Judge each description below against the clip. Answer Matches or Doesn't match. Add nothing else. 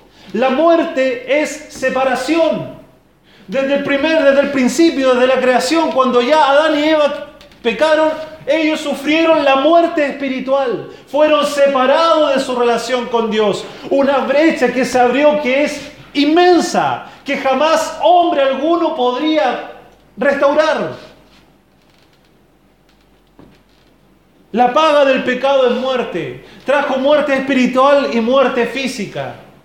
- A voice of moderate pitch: Doesn't match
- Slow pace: Matches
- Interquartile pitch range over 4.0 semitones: Doesn't match